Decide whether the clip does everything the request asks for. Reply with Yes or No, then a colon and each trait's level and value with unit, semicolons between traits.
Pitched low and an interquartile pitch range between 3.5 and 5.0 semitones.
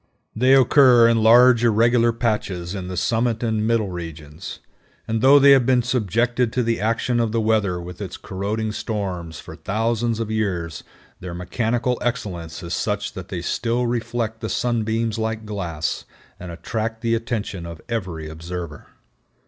Yes: low, 110 Hz; average, 4.3 semitones